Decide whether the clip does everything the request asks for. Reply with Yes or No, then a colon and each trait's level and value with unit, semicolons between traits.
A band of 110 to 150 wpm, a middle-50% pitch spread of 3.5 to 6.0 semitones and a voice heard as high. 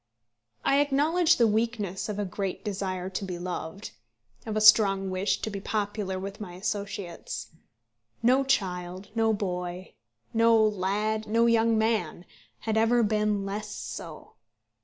No: average, 140 wpm; average, 3.0 semitones; high, 205 Hz